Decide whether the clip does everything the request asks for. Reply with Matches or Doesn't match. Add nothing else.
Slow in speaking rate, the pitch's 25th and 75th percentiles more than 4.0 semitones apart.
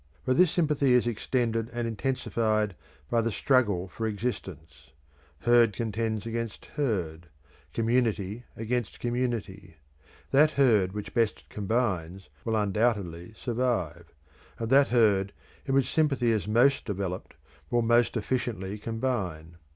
Doesn't match